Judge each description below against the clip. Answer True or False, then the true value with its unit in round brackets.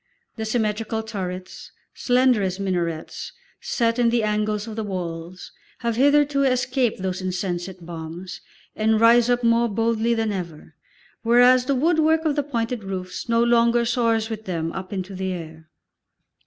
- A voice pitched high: True (220 Hz)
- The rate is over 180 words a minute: False (155 wpm)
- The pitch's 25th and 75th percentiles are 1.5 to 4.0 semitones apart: False (4.4 semitones)